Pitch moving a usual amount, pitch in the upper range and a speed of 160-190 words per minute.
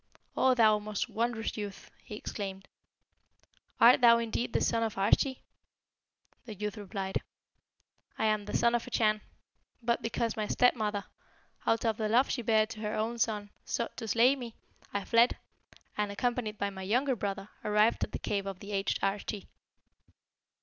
No: narrow, 2.2 semitones; high, 215 Hz; average, 170 wpm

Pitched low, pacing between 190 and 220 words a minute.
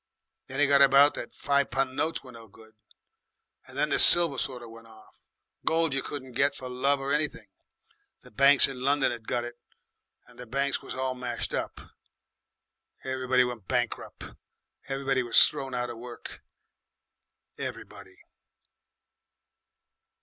No: low, 130 Hz; average, 150 wpm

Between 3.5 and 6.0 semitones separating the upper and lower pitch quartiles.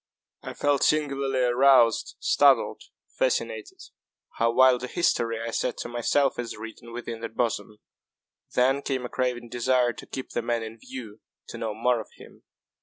No: narrow, 2.4 semitones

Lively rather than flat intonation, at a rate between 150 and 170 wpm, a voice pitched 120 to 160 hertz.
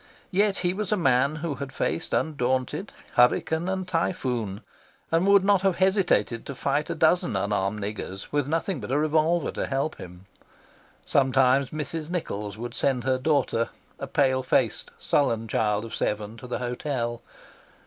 Yes: wide, 5.7 semitones; average, 160 wpm; medium, 140 Hz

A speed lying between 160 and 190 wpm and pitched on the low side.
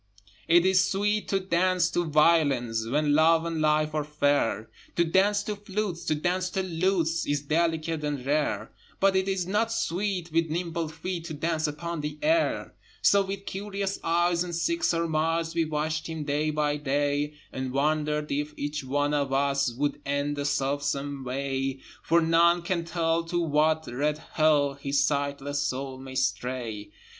No: average, 170 wpm; medium, 155 Hz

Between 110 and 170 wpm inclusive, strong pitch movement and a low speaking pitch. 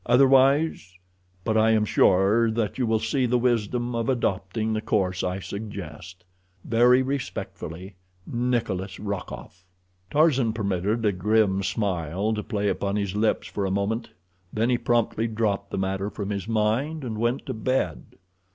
No: average, 150 wpm; average, 3.4 semitones; low, 110 Hz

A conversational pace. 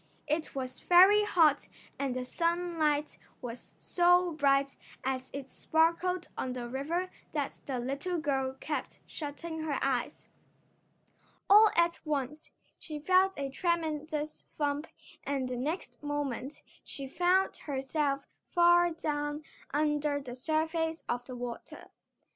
No: slow, 125 wpm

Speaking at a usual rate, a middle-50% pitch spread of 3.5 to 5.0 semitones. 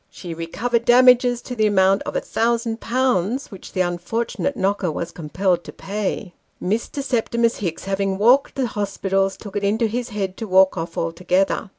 Yes: average, 165 wpm; average, 3.9 semitones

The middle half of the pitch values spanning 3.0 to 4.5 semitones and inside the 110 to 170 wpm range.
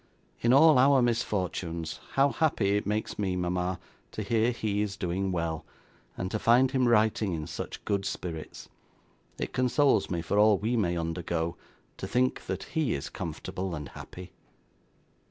No: average, 5.2 semitones; average, 160 wpm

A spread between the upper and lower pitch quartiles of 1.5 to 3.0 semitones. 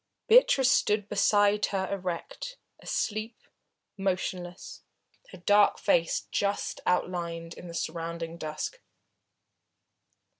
No: average, 3.6 semitones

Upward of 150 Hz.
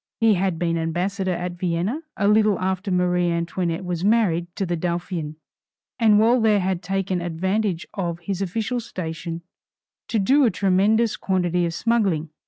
Yes: medium, 185 Hz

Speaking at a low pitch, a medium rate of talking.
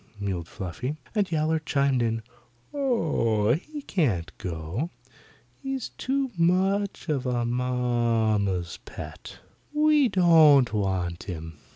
No: low, 125 Hz; slow, 105 wpm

